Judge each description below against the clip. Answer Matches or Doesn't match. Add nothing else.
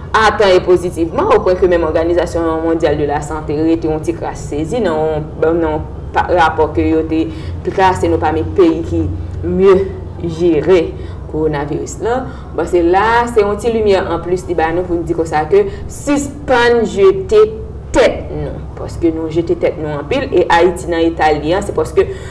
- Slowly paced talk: Doesn't match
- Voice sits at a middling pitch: Matches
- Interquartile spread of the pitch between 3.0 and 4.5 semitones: Matches